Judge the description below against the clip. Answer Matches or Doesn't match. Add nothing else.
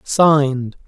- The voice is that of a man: Matches